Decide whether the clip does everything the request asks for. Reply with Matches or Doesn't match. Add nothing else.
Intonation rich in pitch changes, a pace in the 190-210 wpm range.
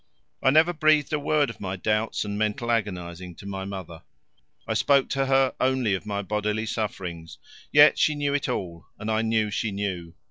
Matches